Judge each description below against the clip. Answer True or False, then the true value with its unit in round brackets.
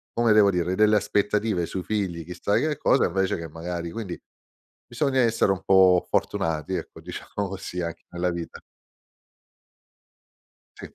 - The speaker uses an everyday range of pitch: True (3.5 semitones)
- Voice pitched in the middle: False (95 Hz)